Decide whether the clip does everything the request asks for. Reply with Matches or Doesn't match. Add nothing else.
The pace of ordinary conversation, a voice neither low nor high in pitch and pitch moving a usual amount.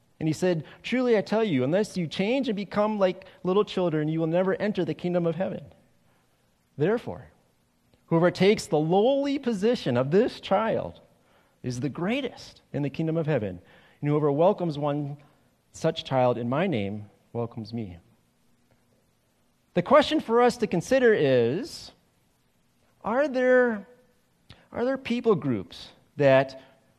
Doesn't match